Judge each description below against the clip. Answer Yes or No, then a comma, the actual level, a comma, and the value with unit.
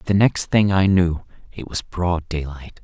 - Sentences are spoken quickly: No, average, 190 wpm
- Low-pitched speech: Yes, very low, 90 Hz